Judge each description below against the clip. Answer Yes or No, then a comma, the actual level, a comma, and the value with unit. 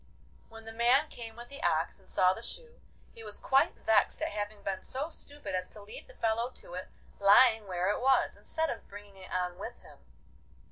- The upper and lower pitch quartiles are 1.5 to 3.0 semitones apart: No, average, 4.8 semitones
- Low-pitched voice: No, high, 225 Hz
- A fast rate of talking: Yes, fast, 215 wpm